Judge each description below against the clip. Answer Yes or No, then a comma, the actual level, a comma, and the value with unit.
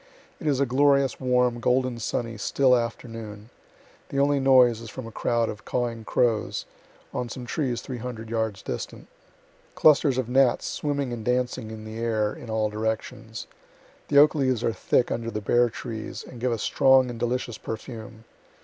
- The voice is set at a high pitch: No, low, 120 Hz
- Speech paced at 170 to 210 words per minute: Yes, average, 175 wpm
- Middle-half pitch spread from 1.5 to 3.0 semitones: Yes, narrow, 2.5 semitones